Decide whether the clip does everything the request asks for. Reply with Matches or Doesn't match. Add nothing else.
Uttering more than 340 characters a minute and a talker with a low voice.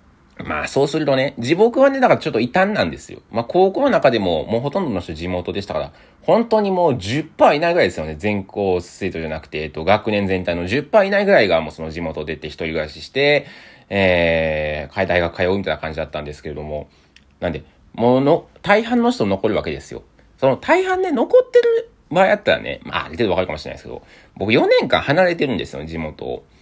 Matches